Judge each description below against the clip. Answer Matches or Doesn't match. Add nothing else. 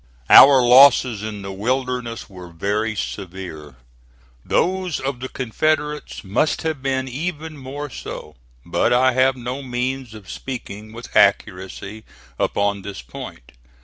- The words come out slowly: Matches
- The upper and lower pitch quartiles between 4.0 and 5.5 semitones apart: Matches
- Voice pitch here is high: Doesn't match